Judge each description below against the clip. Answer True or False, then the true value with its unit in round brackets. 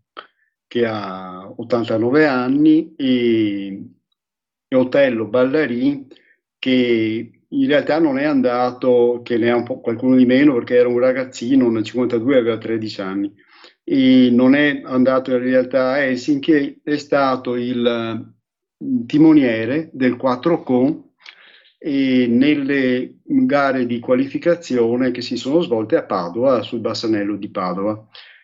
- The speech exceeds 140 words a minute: False (120 wpm)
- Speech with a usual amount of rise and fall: True (4.1 semitones)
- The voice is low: True (125 Hz)